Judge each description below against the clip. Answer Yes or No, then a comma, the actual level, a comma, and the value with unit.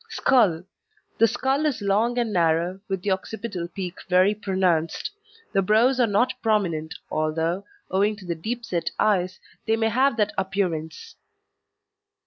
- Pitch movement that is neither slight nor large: Yes, average, 4.2 semitones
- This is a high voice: Yes, high, 195 Hz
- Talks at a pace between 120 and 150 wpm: Yes, average, 145 wpm